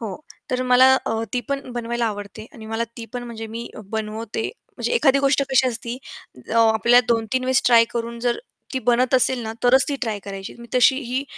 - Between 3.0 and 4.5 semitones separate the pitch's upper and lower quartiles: No, narrow, 2.4 semitones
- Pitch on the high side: Yes, high, 240 Hz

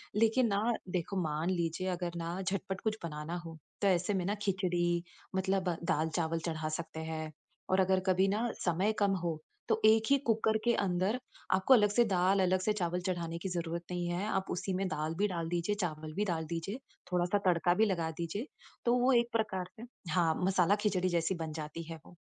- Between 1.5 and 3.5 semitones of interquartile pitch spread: Yes, average, 3.0 semitones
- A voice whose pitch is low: No, medium, 185 Hz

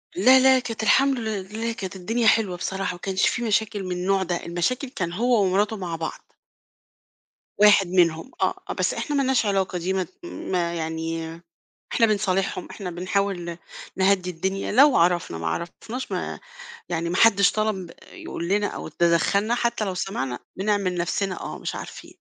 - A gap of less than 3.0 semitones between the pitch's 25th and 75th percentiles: No, average, 3.8 semitones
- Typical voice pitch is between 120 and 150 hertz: No, high, 190 Hz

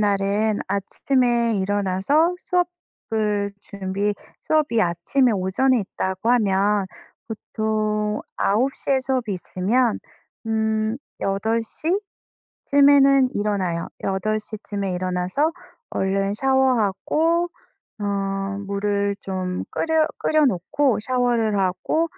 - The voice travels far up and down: No, average, 4.8 semitones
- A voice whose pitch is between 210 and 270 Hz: Yes, high, 215 Hz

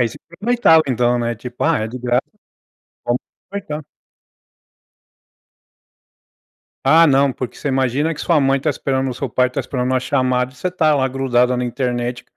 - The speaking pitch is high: No, low, 130 Hz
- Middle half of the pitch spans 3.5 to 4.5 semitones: No, average, 2.7 semitones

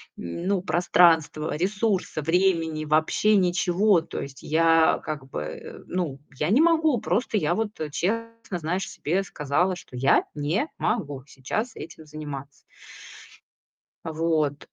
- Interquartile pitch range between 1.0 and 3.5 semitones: No, average, 4.5 semitones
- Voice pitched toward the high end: No, medium, 165 Hz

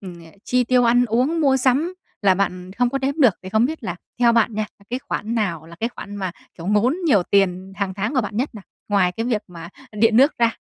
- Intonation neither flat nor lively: Yes, average, 4.4 semitones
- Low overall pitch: No, high, 220 Hz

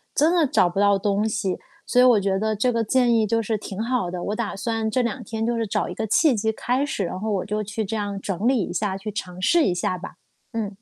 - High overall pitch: Yes, high, 215 Hz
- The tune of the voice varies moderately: Yes, average, 3.0 semitones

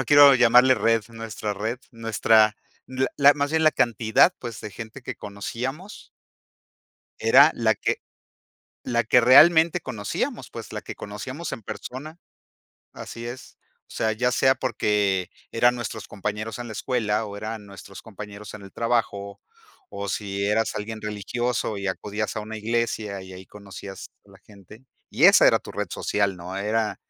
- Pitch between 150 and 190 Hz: No, low, 110 Hz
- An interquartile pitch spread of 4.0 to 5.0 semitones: No, average, 3.1 semitones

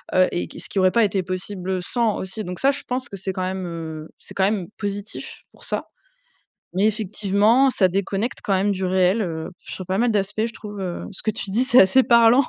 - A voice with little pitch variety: No, average, 3.0 semitones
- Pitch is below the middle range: No, high, 195 Hz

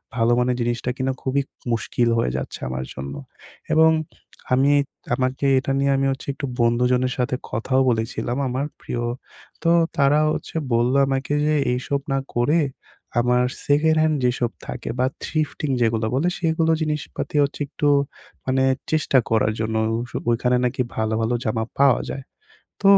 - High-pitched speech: No, low, 130 Hz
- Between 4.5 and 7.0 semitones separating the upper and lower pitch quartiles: No, average, 2.9 semitones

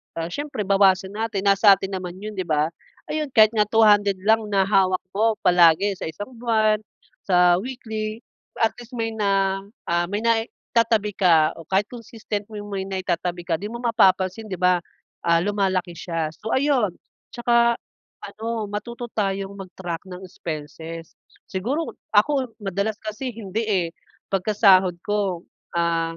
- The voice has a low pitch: No, high, 200 Hz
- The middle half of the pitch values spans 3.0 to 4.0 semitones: Yes, average, 3.4 semitones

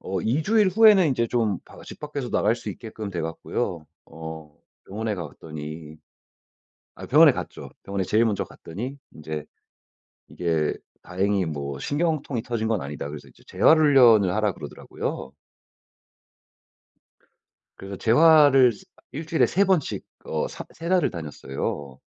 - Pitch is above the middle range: No, low, 105 Hz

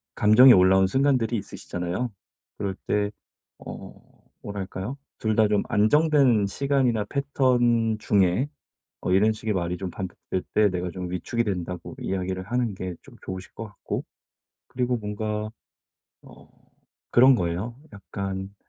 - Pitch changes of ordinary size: Yes, average, 4.3 semitones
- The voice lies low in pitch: Yes, low, 105 Hz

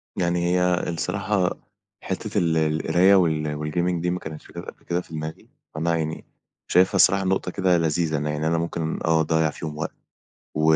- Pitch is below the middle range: Yes, very low, 85 Hz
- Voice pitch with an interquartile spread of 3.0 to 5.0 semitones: No, narrow, 2.4 semitones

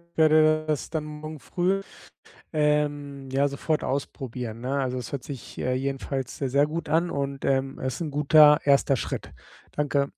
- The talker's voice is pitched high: No, medium, 140 Hz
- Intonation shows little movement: Yes, narrow, 2.2 semitones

